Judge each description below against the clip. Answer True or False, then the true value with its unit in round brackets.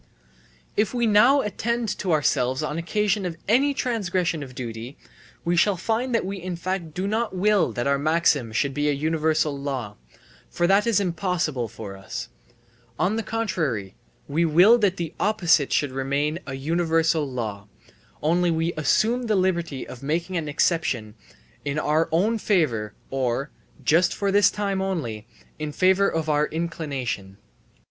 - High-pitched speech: False (165 Hz)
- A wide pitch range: True (5.7 semitones)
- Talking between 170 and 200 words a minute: False (160 wpm)